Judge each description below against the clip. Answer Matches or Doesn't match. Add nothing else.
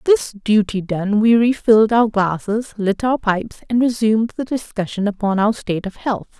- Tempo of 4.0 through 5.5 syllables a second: Matches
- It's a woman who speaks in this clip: Matches